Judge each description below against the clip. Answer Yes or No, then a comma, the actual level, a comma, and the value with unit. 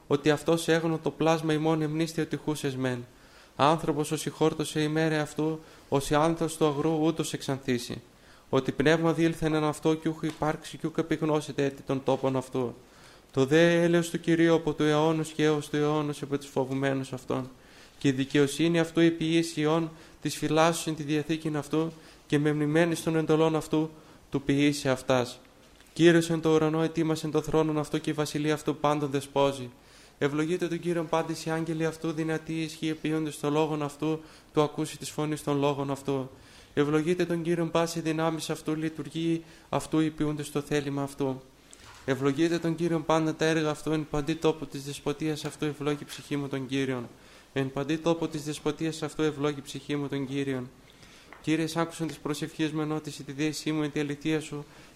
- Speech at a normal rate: No, fast, 180 wpm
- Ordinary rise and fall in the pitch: No, narrow, 2.0 semitones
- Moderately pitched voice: Yes, medium, 155 Hz